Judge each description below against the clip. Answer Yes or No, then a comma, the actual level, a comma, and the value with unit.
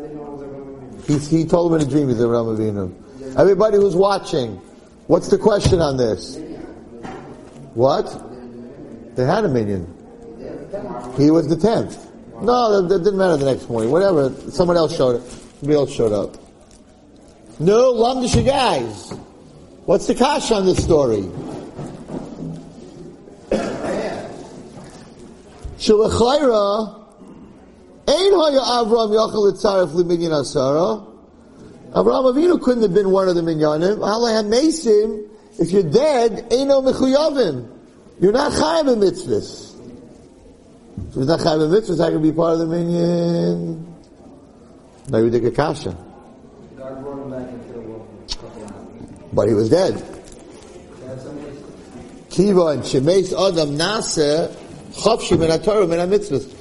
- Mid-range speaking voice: Yes, medium, 170 Hz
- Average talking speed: No, slow, 120 wpm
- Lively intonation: Yes, wide, 7.9 semitones